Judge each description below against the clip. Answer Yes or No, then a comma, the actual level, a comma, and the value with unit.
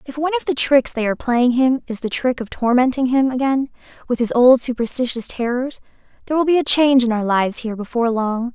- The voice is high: Yes, very high, 250 Hz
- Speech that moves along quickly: Yes, fast, 225 wpm